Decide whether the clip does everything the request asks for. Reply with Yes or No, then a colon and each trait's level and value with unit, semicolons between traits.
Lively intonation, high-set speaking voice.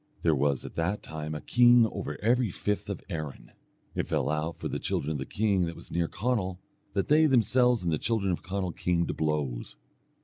No: wide, 6.3 semitones; very low, 90 Hz